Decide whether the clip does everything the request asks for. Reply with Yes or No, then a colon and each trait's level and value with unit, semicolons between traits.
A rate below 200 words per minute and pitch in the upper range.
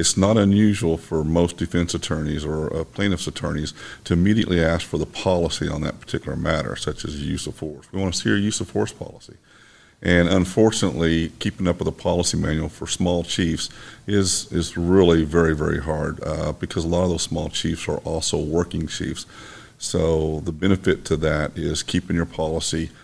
No: average, 190 wpm; very low, 85 Hz